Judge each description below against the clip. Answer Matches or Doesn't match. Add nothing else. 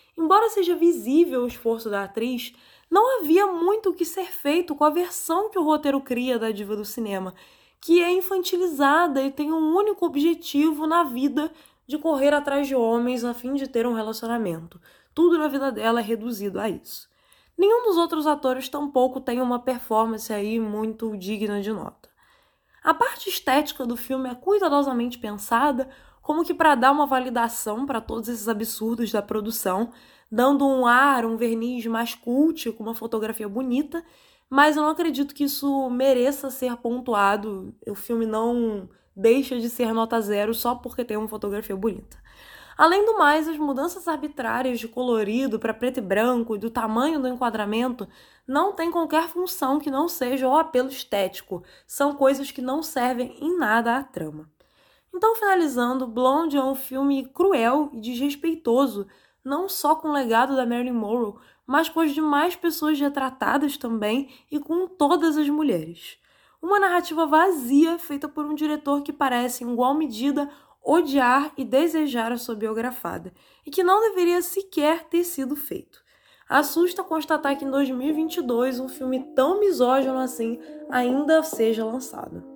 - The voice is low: Doesn't match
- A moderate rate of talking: Matches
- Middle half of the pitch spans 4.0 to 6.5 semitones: Matches